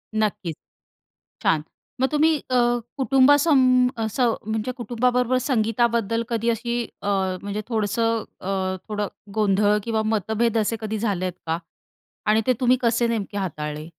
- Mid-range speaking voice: No, high, 225 Hz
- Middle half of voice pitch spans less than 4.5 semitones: Yes, average, 3.1 semitones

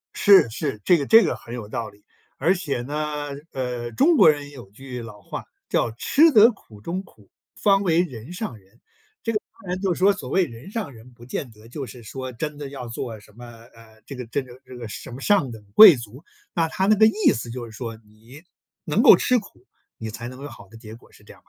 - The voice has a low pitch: Yes, low, 130 Hz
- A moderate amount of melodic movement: No, wide, 7.6 semitones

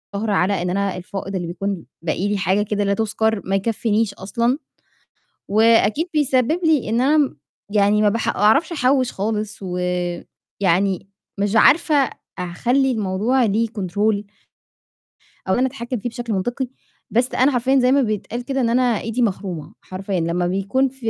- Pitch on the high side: Yes, high, 215 Hz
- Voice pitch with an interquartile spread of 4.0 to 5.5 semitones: Yes, average, 4.3 semitones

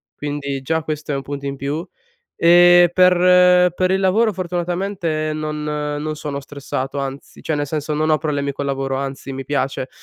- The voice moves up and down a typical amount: Yes, average, 3.9 semitones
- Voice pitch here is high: No, medium, 155 Hz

